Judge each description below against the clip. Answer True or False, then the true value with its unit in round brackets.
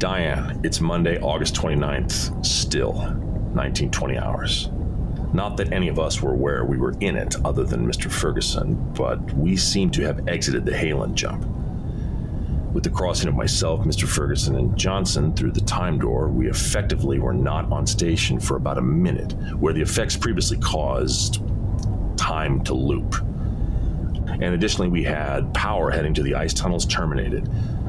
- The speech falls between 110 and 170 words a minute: True (160 wpm)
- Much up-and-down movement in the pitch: True (5.7 semitones)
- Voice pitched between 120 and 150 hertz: False (85 Hz)